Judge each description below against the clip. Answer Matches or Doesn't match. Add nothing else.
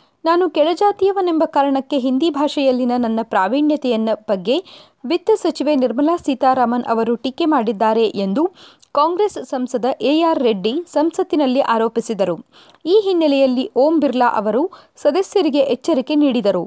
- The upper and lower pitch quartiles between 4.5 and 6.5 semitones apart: Matches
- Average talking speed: Doesn't match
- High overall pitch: Matches